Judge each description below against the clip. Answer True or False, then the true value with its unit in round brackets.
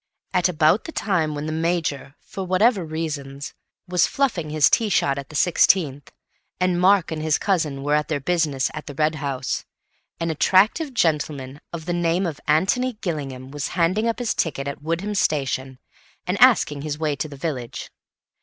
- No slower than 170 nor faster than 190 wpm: True (180 wpm)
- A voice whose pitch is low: False (155 Hz)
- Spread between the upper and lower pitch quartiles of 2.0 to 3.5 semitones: False (4.1 semitones)